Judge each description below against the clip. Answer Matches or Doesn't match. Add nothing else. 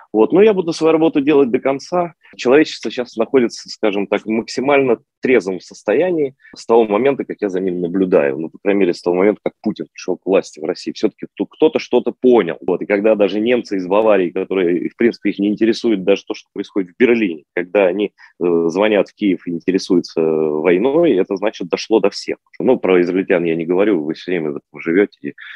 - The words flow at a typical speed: Doesn't match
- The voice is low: Matches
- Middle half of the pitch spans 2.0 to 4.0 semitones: Doesn't match